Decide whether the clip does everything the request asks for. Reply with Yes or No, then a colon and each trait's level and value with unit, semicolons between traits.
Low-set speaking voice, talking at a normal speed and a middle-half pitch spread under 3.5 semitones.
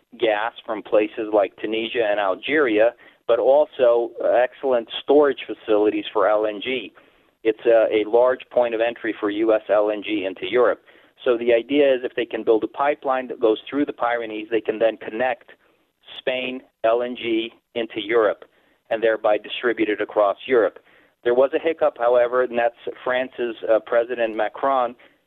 Yes: low, 120 Hz; average, 155 wpm; average, 2.7 semitones